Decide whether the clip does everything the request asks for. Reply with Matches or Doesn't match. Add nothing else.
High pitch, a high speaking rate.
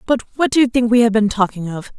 Matches